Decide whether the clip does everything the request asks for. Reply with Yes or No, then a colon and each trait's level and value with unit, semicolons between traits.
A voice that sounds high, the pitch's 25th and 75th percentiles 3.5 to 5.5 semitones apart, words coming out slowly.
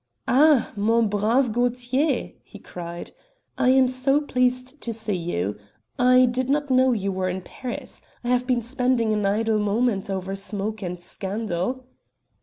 No: high, 235 Hz; average, 4.3 semitones; average, 155 wpm